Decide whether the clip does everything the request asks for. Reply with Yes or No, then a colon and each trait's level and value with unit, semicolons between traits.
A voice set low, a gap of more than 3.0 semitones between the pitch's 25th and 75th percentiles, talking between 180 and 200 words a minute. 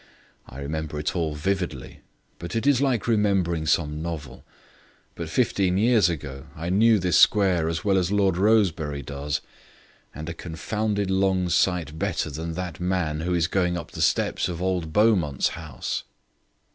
No: very low, 85 Hz; average, 3.7 semitones; average, 160 wpm